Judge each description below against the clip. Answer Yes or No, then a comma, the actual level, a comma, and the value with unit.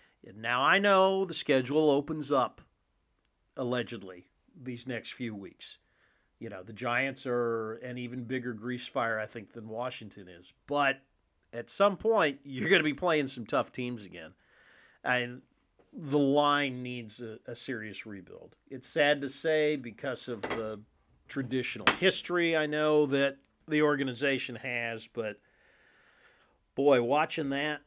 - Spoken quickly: No, average, 145 wpm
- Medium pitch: No, low, 125 Hz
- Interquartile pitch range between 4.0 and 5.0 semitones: Yes, average, 4.3 semitones